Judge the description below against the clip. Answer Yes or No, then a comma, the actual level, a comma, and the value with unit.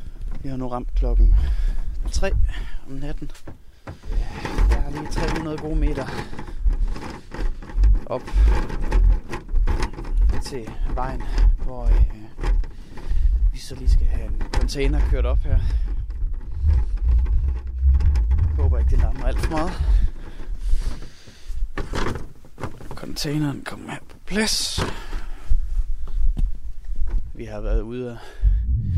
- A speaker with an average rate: No, slow, 95 wpm